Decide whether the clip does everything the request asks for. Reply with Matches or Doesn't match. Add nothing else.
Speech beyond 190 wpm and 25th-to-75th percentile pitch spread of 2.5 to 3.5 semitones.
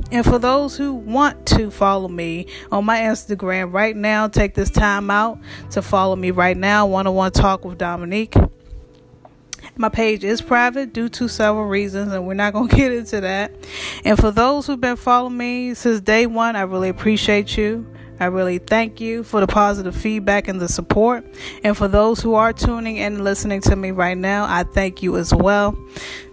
Matches